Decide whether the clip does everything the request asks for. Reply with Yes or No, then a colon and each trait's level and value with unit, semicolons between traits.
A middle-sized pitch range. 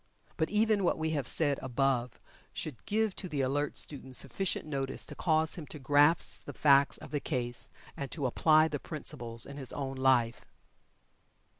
Yes: average, 3.1 semitones